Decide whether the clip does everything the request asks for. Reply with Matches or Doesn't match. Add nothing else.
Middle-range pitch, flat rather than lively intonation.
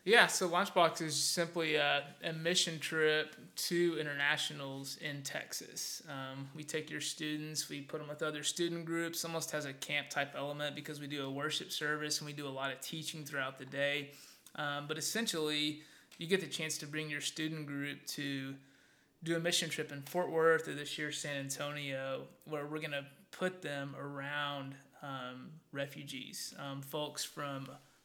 Matches